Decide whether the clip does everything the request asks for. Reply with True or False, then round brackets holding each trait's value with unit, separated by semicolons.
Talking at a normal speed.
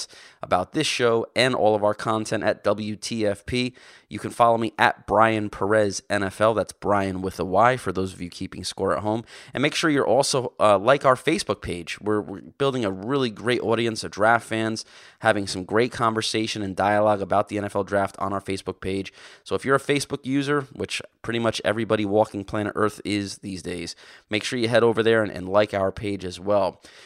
False (210 wpm)